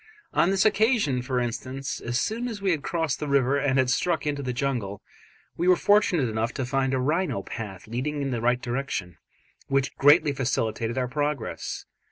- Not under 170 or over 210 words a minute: Yes, average, 190 wpm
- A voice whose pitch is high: No, low, 135 Hz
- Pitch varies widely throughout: No, average, 3.5 semitones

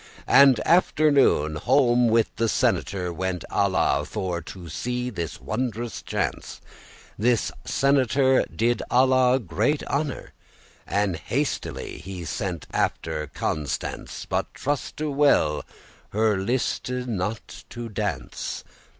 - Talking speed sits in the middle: No, slow, 110 wpm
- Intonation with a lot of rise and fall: Yes, wide, 5.9 semitones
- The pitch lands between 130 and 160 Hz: No, low, 115 Hz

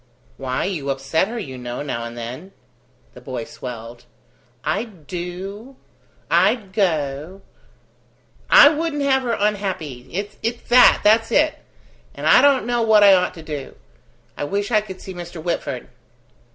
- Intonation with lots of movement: Yes, wide, 7.8 semitones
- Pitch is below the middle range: No, high, 190 Hz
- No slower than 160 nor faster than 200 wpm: No, average, 150 wpm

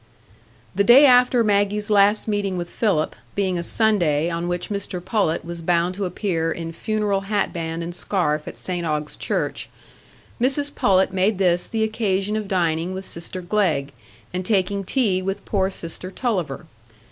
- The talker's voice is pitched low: No, high, 190 Hz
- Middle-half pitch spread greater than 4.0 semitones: No, average, 3.3 semitones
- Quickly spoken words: No, average, 160 wpm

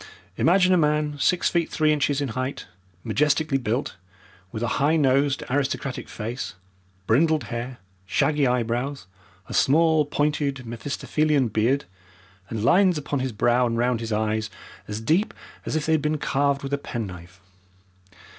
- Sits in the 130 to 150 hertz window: Yes, medium, 140 Hz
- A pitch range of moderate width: Yes, average, 4.2 semitones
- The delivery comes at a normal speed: Yes, average, 150 wpm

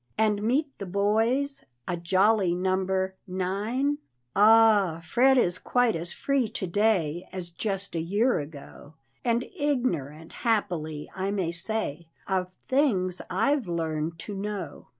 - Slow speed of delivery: Yes, slow, 130 wpm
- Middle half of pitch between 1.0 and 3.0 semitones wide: No, average, 4.6 semitones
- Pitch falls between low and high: No, high, 195 Hz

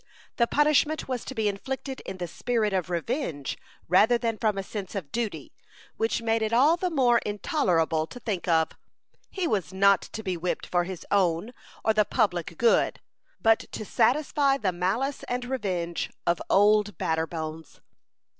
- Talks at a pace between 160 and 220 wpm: Yes, average, 165 wpm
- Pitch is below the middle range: No, high, 210 Hz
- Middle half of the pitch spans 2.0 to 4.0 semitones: No, wide, 5.4 semitones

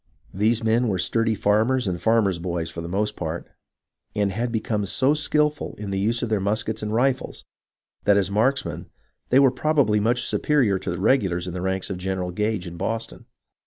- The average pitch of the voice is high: No, low, 105 Hz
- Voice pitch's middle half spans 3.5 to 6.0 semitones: Yes, average, 4.0 semitones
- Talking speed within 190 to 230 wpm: Yes, average, 200 wpm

